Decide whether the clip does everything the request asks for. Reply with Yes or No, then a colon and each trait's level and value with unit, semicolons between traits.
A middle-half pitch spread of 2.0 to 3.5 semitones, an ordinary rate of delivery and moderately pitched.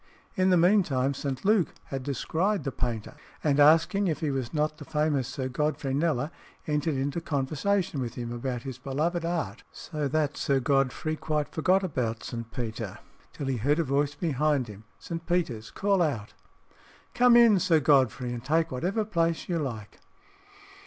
No: average, 4.2 semitones; average, 170 wpm; medium, 145 Hz